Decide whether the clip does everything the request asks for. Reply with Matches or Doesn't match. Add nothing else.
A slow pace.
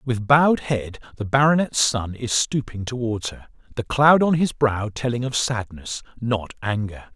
Doesn't match